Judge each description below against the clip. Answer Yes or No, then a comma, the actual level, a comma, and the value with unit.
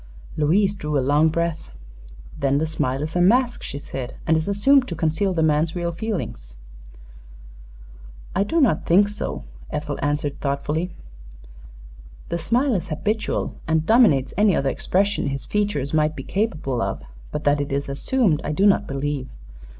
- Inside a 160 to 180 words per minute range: Yes, average, 165 wpm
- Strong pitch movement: Yes, wide, 5.8 semitones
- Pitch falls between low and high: Yes, medium, 160 Hz